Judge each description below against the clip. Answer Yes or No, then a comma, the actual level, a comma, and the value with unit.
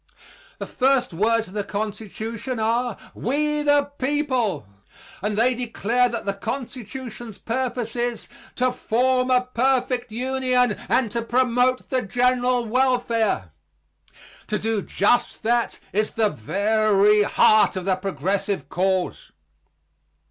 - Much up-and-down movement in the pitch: No, average, 3.1 semitones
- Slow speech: Yes, slow, 120 wpm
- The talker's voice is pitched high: Yes, high, 235 Hz